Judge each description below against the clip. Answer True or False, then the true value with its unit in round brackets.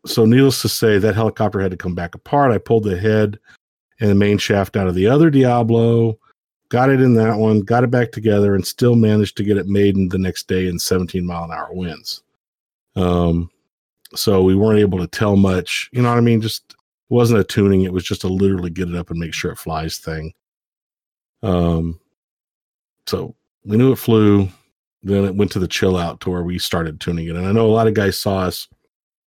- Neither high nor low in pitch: False (100 Hz)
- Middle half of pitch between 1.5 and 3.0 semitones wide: False (3.6 semitones)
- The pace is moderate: False (225 wpm)